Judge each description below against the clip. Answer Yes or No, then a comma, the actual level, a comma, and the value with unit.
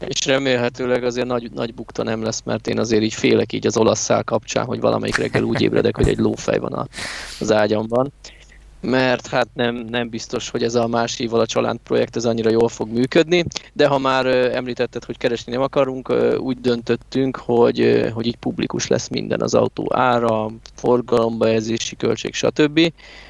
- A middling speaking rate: No, fast, 180 wpm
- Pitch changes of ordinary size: No, narrow, 2.0 semitones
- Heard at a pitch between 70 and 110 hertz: No, low, 120 Hz